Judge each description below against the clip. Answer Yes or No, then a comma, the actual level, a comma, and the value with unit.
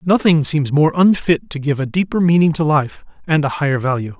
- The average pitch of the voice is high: No, medium, 155 Hz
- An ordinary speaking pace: No, fast, 215 wpm